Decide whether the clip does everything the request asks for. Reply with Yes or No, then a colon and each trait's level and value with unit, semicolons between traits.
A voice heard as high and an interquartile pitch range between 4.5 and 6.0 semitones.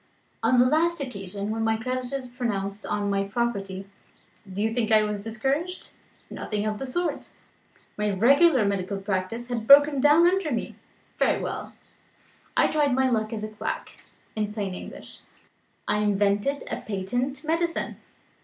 Yes: high, 225 Hz; average, 5.1 semitones